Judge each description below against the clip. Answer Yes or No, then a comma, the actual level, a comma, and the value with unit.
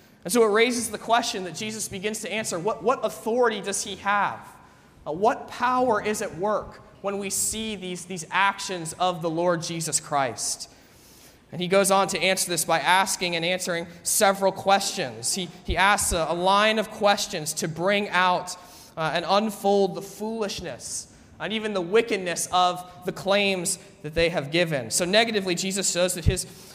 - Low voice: No, high, 190 Hz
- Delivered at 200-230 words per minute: No, average, 180 wpm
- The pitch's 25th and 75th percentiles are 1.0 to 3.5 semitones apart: Yes, average, 2.8 semitones